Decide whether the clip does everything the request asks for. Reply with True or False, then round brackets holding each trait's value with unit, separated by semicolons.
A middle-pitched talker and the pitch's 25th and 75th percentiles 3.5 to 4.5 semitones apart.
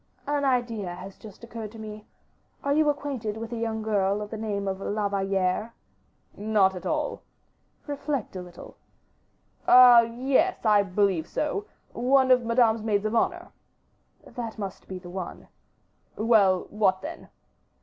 False (220 Hz; 3.8 semitones)